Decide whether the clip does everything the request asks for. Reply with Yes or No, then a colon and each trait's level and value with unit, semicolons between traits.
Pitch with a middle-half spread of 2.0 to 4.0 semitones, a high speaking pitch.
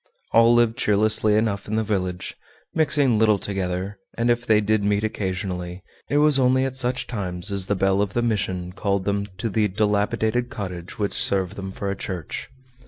No: average, 3.0 semitones; low, 105 Hz